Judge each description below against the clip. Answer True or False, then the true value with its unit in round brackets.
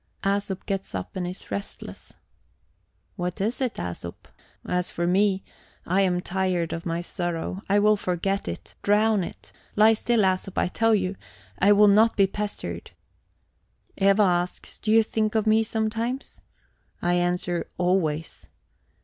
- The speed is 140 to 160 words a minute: True (150 wpm)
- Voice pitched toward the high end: True (195 Hz)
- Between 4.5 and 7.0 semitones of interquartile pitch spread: False (3.1 semitones)